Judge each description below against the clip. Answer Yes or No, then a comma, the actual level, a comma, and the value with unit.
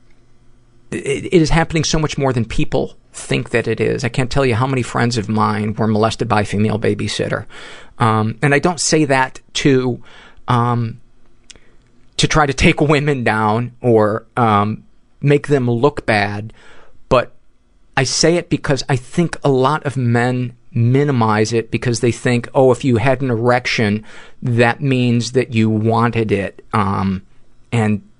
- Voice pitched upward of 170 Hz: No, low, 120 Hz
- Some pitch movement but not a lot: Yes, average, 3.2 semitones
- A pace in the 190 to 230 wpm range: No, average, 165 wpm